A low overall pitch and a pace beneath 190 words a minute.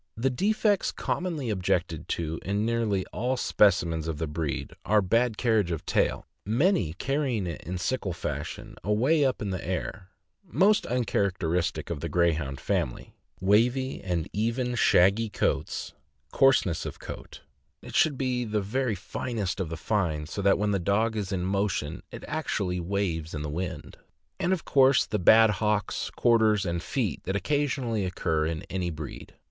Yes: low, 100 Hz; average, 165 wpm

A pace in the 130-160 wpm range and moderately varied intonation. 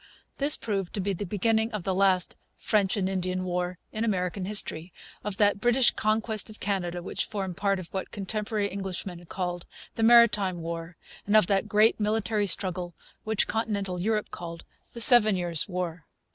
No: average, 175 wpm; average, 3.0 semitones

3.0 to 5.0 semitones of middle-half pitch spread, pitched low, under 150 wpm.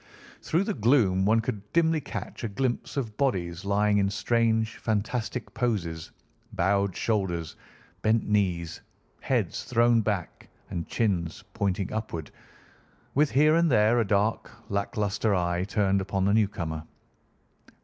Yes: average, 3.4 semitones; low, 105 Hz; slow, 135 wpm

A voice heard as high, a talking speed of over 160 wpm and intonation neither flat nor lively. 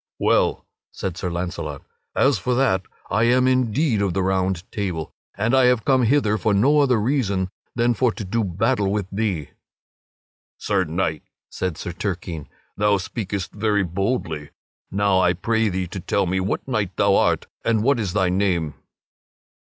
No: low, 100 Hz; average, 170 wpm; average, 4.0 semitones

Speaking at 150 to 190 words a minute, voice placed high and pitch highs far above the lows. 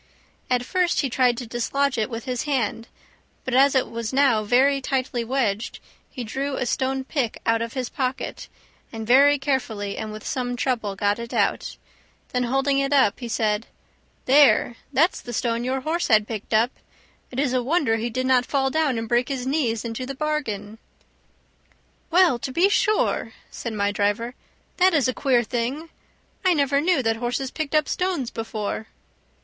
No: average, 180 wpm; very high, 255 Hz; average, 3.3 semitones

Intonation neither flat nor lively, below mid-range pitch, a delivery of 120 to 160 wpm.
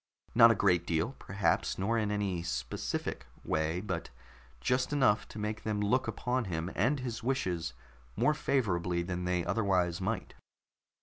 Yes: average, 4.7 semitones; low, 100 Hz; average, 150 wpm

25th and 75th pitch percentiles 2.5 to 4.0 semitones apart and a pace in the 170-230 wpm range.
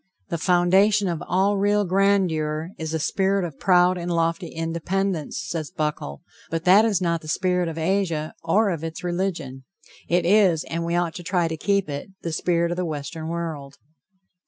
Yes: average, 2.8 semitones; average, 180 wpm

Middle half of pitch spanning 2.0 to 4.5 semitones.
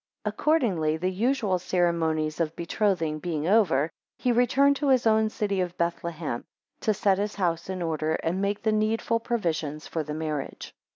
No: average, 5.2 semitones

